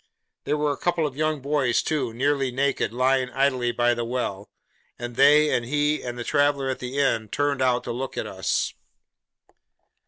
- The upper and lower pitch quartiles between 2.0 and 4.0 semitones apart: Yes, average, 2.9 semitones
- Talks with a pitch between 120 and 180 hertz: Yes, low, 135 Hz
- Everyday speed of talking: Yes, average, 185 wpm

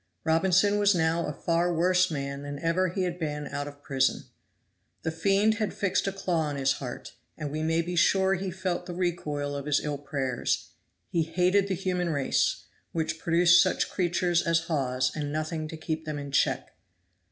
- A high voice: No, medium, 165 Hz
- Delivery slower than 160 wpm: No, average, 190 wpm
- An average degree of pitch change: Yes, average, 3.5 semitones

